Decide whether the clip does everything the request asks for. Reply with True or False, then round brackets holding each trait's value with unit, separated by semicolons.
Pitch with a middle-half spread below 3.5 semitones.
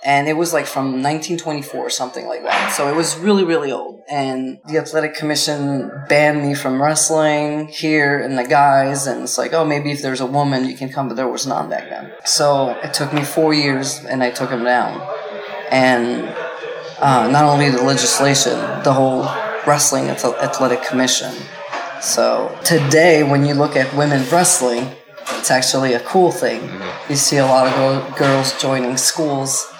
True (2.5 semitones)